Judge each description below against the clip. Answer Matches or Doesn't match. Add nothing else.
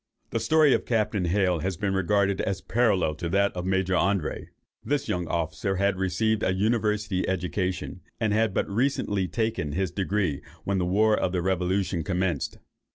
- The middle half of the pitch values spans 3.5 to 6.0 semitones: Doesn't match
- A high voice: Doesn't match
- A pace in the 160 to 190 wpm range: Matches